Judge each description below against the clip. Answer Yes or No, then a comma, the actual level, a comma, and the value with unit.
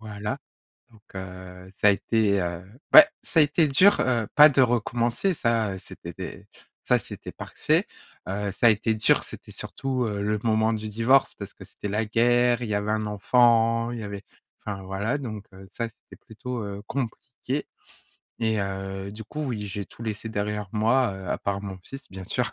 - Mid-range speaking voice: No, low, 110 Hz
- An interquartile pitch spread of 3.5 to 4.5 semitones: No, average, 3.1 semitones